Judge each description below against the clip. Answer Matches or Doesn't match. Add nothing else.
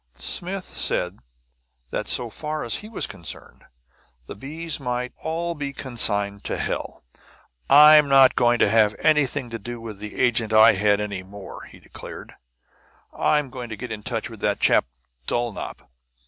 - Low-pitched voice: Matches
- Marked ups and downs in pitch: Matches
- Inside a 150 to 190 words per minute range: Matches